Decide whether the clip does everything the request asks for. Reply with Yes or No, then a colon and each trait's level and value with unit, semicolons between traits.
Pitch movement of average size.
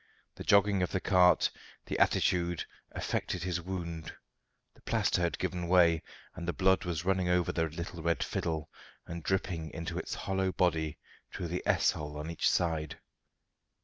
No: narrow, 1.9 semitones